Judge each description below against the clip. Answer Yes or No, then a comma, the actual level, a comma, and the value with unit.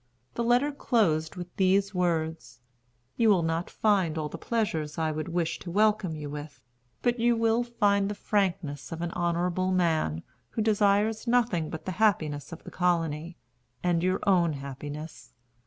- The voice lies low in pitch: No, medium, 180 Hz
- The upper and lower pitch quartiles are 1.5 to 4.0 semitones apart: No, average, 4.6 semitones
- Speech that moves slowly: No, average, 165 wpm